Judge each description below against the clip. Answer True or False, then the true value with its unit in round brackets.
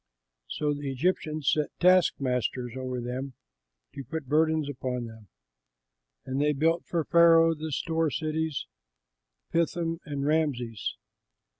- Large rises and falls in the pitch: False (3.8 semitones)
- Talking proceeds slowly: True (120 wpm)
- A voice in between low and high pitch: True (150 Hz)